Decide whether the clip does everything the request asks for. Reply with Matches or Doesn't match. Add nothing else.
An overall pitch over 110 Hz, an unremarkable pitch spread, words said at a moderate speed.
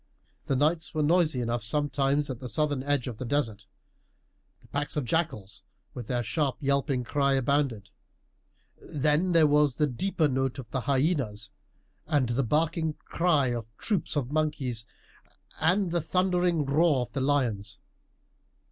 Matches